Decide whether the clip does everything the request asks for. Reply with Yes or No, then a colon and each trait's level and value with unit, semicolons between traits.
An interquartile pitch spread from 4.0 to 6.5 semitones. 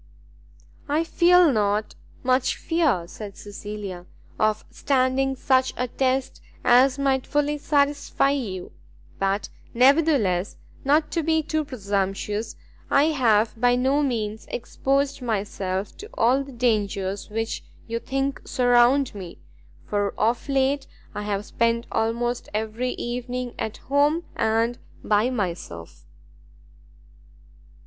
Yes: average, 4.6 semitones